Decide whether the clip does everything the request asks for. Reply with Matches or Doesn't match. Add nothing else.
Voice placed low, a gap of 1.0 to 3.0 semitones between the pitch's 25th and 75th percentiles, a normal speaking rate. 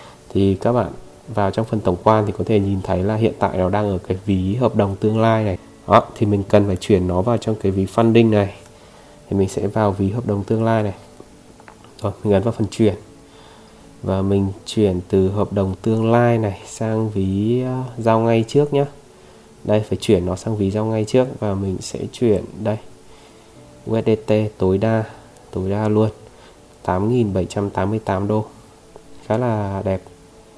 Matches